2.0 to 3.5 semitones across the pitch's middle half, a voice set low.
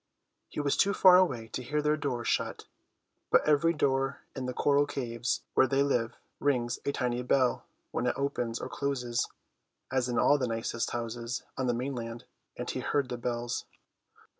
Yes: average, 2.9 semitones; low, 130 Hz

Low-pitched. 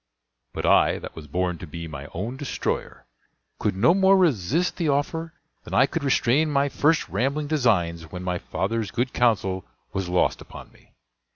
Yes: low, 120 Hz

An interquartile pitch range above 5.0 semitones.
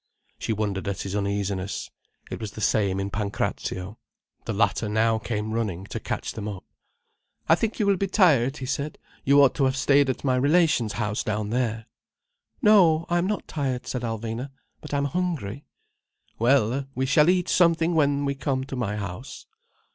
Yes: wide, 5.4 semitones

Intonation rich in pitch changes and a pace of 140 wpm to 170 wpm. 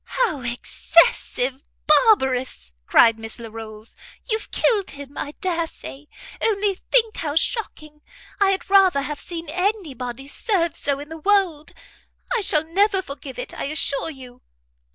Yes: wide, 6.5 semitones; average, 145 wpm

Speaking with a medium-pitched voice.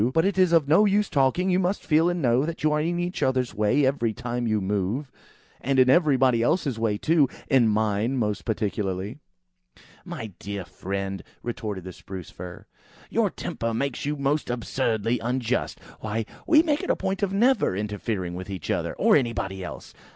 No: low, 125 Hz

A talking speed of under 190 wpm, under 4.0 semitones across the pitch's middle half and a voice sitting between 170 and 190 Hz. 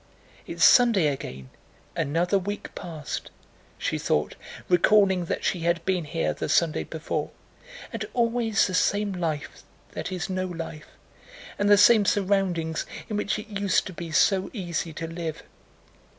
Yes: average, 145 wpm; average, 3.6 semitones; medium, 185 Hz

